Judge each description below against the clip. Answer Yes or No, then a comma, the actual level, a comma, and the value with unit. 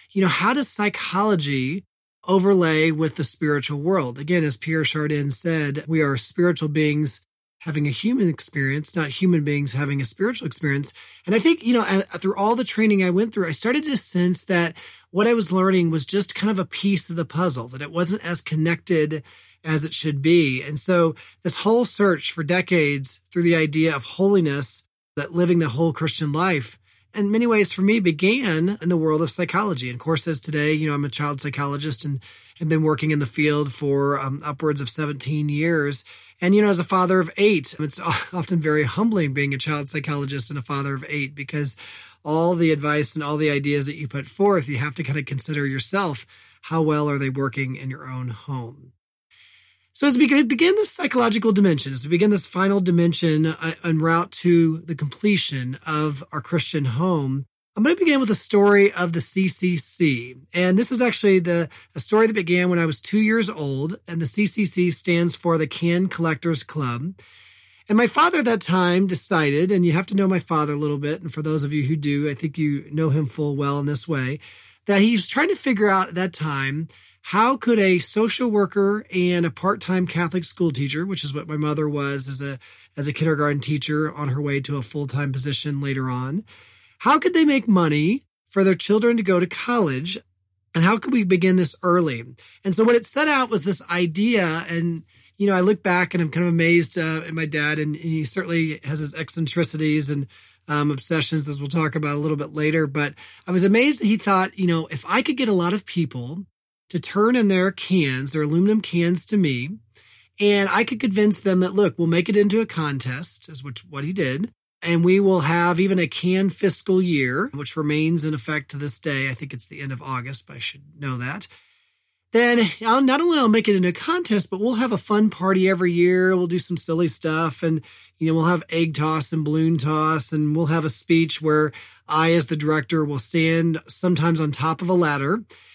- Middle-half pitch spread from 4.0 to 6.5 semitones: Yes, average, 4.5 semitones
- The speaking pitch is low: No, medium, 165 Hz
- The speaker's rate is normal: No, fast, 215 wpm